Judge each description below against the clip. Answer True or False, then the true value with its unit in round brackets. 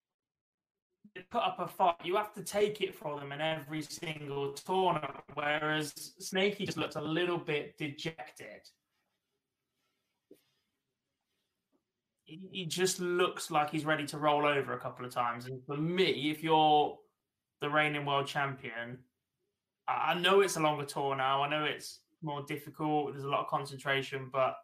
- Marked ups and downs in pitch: False (3.7 semitones)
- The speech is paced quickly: False (155 wpm)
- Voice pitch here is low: False (150 Hz)